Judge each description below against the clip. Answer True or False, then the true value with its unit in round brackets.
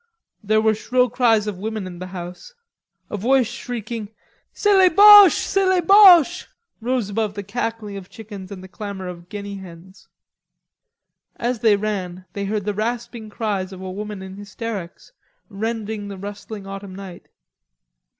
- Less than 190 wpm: True (160 wpm)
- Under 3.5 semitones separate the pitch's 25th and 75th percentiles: True (3.1 semitones)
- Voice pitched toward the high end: True (210 Hz)